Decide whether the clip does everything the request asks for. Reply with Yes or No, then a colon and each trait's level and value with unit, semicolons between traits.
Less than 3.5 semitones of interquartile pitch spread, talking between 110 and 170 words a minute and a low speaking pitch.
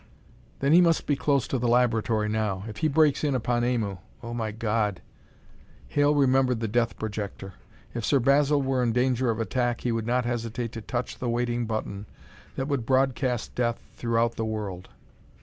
No: average, 2.9 semitones; average, 185 wpm; low, 120 Hz